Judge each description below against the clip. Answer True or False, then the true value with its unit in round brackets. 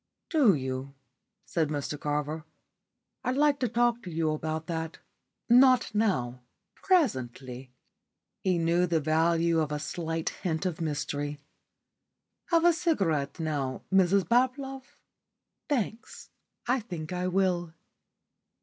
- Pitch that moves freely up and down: True (7.4 semitones)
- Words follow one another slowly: True (120 wpm)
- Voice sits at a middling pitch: True (170 Hz)